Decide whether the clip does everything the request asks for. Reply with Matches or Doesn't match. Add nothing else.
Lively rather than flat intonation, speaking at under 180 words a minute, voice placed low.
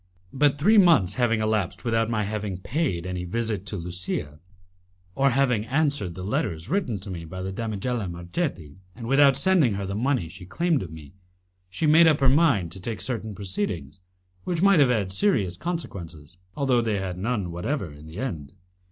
Doesn't match